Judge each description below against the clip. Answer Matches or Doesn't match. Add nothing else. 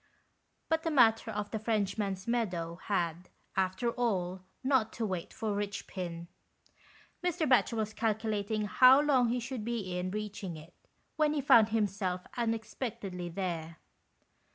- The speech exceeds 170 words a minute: Doesn't match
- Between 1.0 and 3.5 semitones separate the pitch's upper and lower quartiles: Doesn't match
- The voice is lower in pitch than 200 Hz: Doesn't match